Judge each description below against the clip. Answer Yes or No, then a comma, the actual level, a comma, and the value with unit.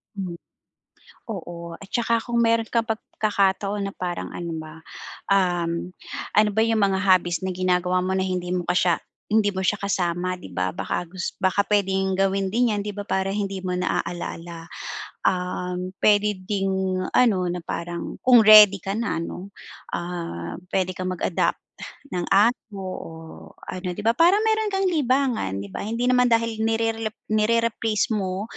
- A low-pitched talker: No, high, 195 Hz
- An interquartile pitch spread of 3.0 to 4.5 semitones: Yes, average, 3.5 semitones